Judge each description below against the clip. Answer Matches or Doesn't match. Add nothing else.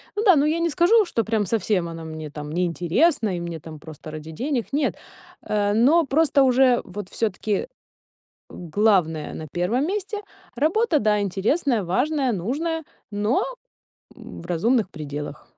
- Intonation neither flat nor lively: Doesn't match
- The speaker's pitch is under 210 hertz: Doesn't match